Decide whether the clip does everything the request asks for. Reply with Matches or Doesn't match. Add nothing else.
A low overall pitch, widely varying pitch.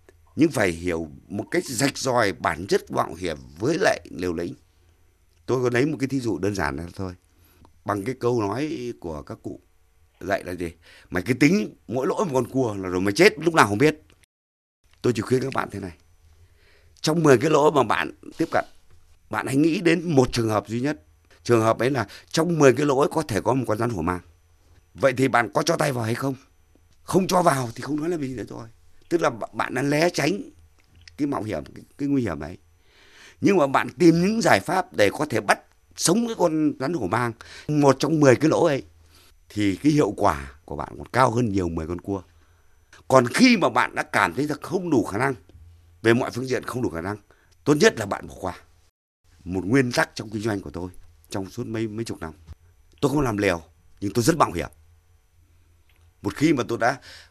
Matches